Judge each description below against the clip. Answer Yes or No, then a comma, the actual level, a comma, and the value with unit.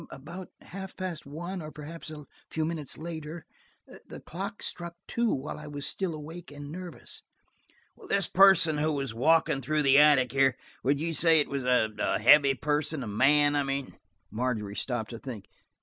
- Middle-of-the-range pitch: Yes, medium, 150 Hz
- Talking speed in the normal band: Yes, average, 170 wpm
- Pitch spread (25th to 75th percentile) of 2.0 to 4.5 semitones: Yes, average, 3.4 semitones